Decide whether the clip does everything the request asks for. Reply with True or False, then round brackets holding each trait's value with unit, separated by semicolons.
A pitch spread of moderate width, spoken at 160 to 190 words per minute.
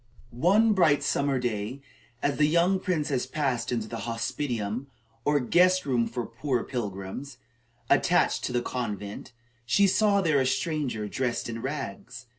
False (4.4 semitones; 145 wpm)